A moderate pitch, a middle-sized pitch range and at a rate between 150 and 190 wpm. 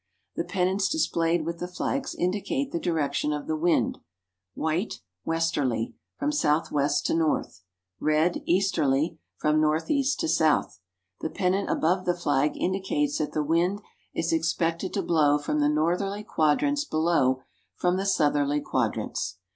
No: medium, 165 Hz; average, 3.9 semitones; average, 140 wpm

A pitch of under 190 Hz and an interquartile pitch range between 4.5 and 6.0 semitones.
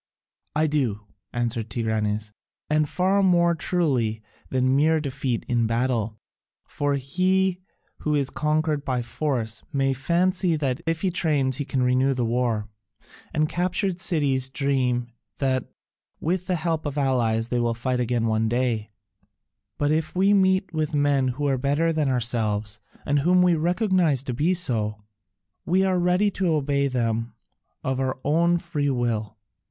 Yes: medium, 140 Hz; wide, 5.4 semitones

